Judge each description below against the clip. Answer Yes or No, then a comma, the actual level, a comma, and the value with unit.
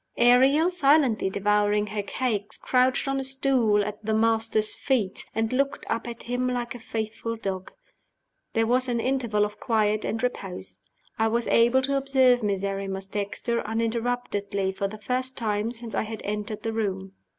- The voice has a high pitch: Yes, high, 225 Hz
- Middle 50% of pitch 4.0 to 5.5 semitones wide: No, average, 3.2 semitones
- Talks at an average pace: Yes, average, 165 wpm